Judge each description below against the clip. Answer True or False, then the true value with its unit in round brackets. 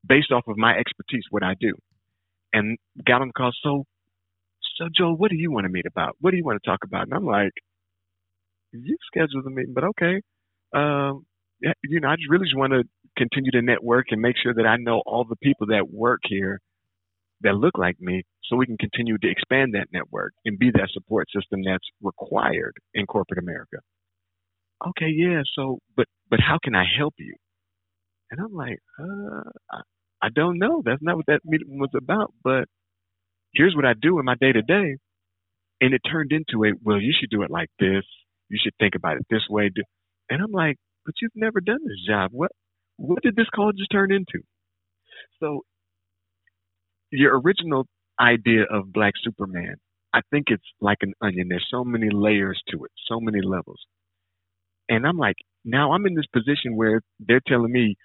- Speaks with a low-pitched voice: True (115 Hz)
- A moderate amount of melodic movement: False (7.7 semitones)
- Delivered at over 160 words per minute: True (195 wpm)